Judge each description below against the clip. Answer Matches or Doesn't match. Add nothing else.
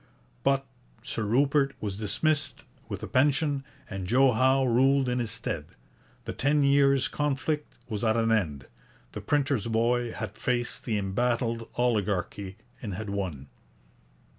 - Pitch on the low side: Matches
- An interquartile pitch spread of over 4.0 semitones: Matches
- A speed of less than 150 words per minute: Matches